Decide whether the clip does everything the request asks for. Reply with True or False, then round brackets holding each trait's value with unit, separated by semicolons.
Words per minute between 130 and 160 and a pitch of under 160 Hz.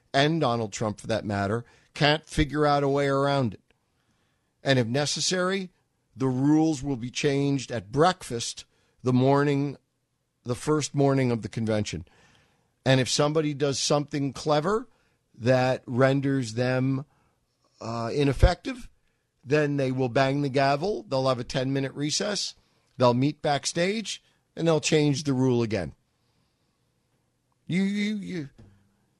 True (135 wpm; 135 Hz)